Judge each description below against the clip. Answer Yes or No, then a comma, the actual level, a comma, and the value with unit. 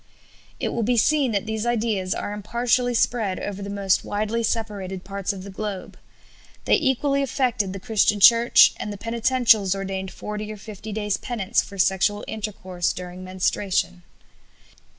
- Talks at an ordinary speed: Yes, average, 160 wpm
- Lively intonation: No, average, 3.1 semitones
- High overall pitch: Yes, high, 210 Hz